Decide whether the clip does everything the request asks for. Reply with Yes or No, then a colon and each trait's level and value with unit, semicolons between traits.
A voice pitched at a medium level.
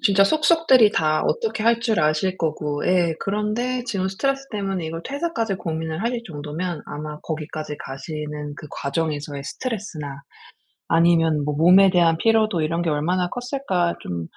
Yes: medium, 175 Hz